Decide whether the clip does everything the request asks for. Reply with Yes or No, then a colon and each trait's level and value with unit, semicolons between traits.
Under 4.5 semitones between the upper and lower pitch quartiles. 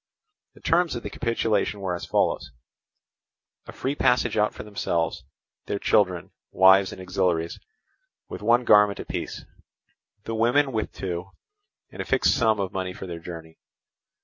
Yes: average, 3.7 semitones